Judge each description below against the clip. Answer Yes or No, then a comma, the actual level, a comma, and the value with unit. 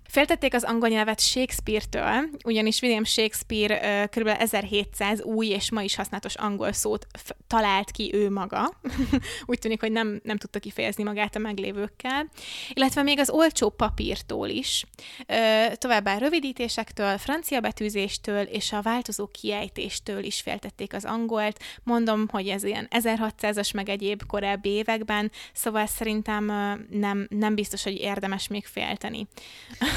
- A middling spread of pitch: No, narrow, 1.9 semitones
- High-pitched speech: Yes, high, 215 Hz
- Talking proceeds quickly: No, average, 140 wpm